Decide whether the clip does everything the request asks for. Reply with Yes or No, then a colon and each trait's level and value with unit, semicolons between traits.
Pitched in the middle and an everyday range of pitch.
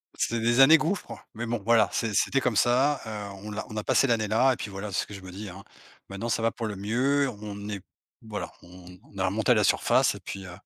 No: low, 110 Hz; average, 3.0 semitones